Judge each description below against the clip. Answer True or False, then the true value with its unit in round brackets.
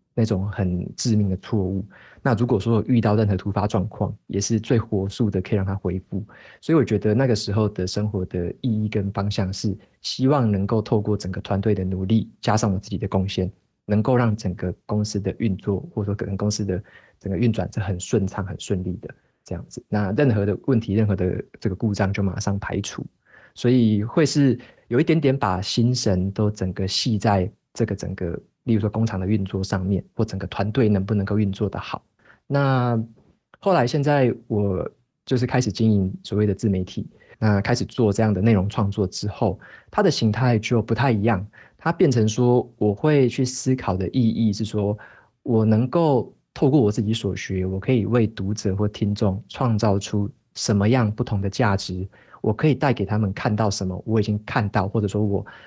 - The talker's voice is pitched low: True (105 Hz)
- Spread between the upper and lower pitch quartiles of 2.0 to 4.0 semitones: True (2.9 semitones)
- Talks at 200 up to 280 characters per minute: False (290 characters per minute)